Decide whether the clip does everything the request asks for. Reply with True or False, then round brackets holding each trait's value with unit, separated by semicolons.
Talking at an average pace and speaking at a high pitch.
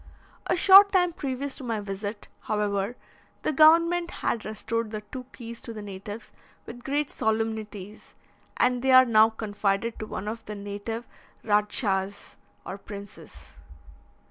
True (145 wpm; 220 Hz)